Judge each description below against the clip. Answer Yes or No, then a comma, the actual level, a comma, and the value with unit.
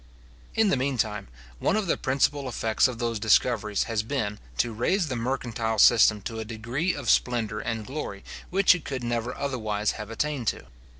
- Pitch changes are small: No, average, 3.7 semitones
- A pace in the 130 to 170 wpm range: No, average, 185 wpm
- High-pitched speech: No, low, 120 Hz